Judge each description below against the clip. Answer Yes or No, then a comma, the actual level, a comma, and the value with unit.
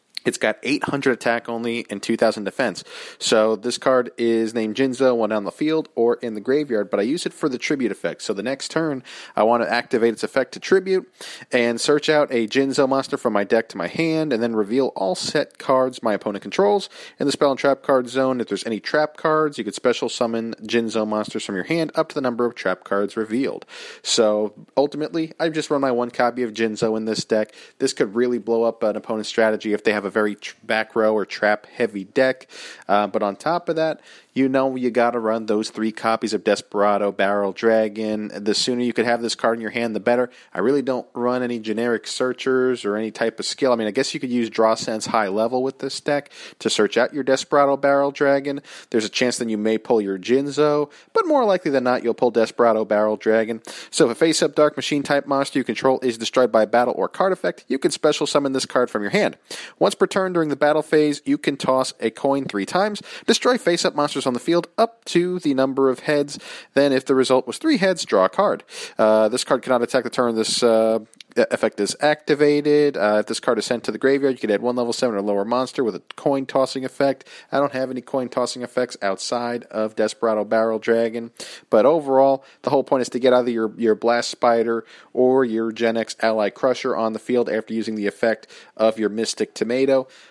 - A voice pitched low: Yes, low, 125 Hz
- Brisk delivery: Yes, fast, 230 wpm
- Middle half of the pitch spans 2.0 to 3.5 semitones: No, average, 3.9 semitones